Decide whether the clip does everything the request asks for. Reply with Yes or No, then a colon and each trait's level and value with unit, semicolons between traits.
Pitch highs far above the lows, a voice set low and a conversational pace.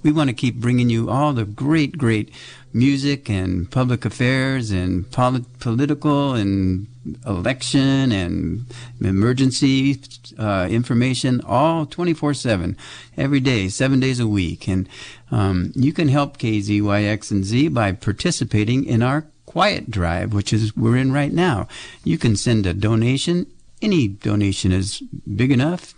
No: average, 4.8 semitones; low, 120 Hz; average, 145 wpm